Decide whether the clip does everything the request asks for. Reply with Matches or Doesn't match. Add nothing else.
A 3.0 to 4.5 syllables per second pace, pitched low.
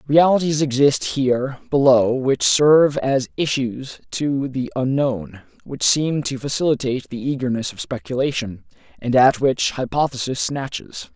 Matches